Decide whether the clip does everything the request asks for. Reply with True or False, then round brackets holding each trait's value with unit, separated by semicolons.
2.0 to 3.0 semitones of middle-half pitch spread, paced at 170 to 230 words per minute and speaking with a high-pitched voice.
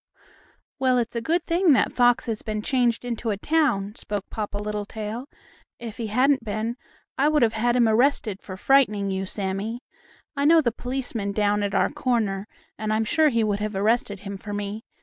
False (3.4 semitones; 190 wpm; 220 Hz)